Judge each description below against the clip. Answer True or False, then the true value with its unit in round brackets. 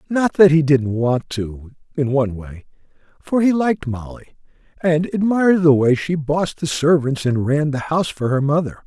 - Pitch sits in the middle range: True (150 Hz)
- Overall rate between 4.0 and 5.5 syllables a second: True (5.0 syllables/s)